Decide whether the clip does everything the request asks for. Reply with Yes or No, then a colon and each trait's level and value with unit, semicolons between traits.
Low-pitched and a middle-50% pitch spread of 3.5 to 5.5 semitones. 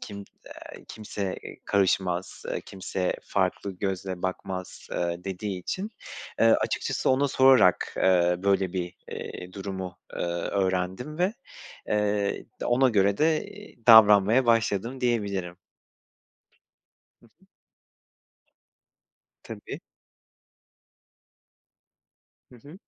Yes: low, 100 Hz; average, 3.9 semitones